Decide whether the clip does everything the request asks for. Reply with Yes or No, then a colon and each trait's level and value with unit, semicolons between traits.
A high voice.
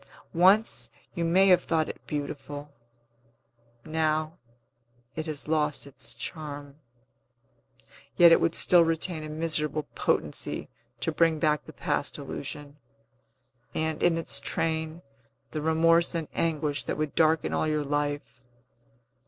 No: medium, 155 Hz